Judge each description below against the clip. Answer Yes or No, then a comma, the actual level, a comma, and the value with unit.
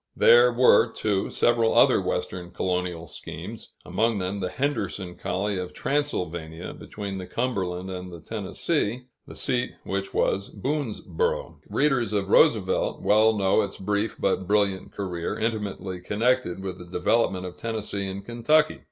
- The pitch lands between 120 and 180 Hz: No, low, 100 Hz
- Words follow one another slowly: No, average, 145 wpm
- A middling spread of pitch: Yes, average, 4.1 semitones